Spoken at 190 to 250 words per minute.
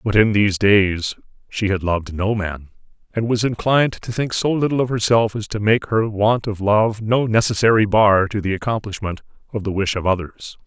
Yes: average, 200 wpm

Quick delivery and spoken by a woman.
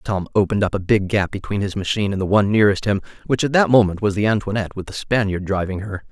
No: fast, 255 wpm; male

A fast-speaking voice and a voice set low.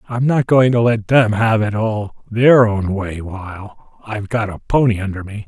Yes: fast, 210 wpm; low, 110 Hz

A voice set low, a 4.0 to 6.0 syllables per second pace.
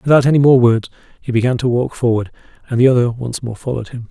No: low, 120 Hz; 6.9 syllables/s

